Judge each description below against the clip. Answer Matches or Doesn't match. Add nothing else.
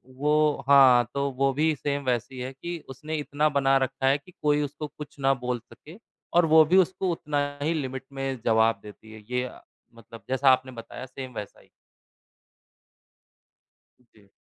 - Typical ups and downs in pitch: Matches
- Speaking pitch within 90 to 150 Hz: Matches